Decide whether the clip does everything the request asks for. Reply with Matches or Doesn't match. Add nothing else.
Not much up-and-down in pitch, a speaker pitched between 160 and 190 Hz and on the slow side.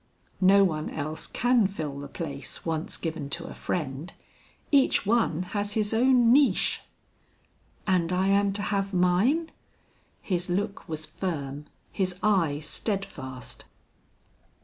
Doesn't match